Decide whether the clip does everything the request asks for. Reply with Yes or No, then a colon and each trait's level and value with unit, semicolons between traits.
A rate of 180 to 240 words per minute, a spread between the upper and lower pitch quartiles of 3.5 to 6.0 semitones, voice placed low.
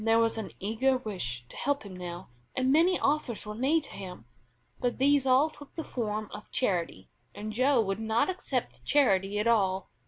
No: average, 190 wpm; average, 5.3 semitones; high, 225 Hz